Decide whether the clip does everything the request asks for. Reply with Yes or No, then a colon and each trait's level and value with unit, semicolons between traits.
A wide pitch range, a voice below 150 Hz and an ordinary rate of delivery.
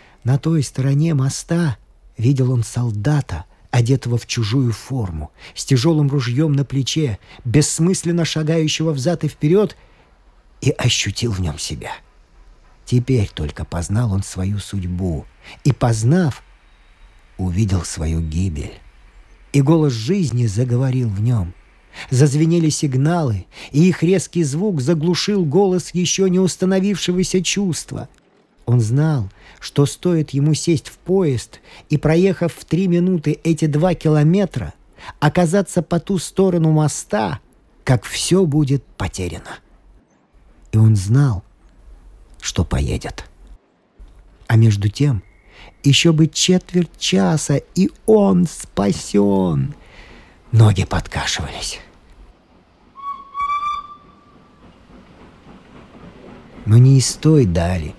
No: wide, 7.7 semitones; medium, 140 Hz; slow, 105 wpm